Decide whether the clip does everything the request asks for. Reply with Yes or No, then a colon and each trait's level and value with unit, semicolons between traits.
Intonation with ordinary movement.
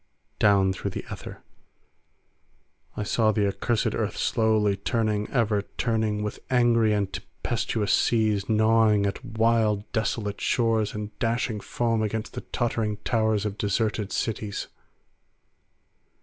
No: narrow, 1.6 semitones